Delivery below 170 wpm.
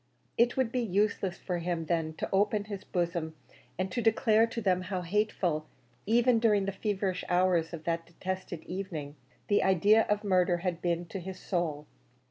No: average, 175 wpm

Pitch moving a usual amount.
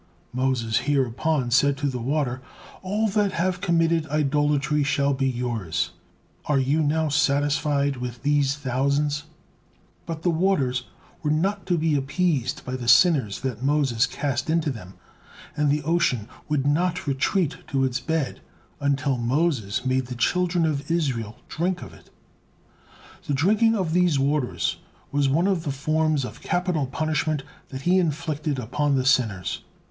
Yes: average, 3.6 semitones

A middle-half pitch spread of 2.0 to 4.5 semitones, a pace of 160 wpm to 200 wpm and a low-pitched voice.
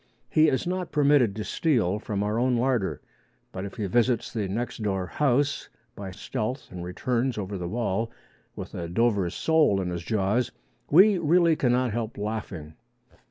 No: average, 5.1 semitones; average, 165 wpm; low, 115 Hz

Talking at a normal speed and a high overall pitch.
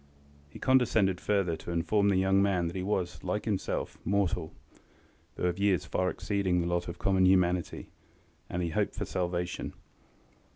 No: average, 170 wpm; very low, 95 Hz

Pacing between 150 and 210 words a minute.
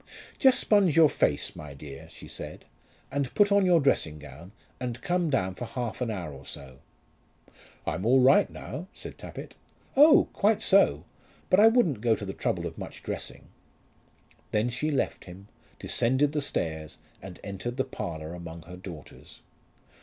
Yes: average, 170 wpm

